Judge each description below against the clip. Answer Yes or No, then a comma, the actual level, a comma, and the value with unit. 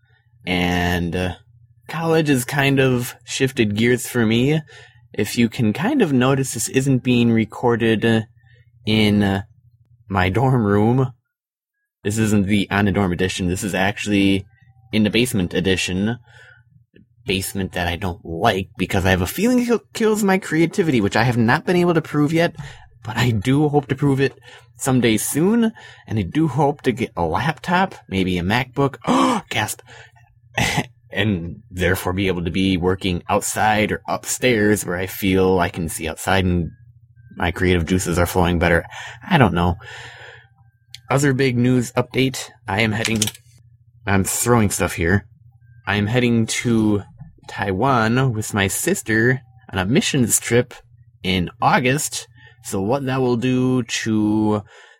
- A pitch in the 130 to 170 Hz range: No, low, 115 Hz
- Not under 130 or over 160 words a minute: Yes, average, 155 wpm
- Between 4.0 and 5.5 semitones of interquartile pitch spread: Yes, average, 4.3 semitones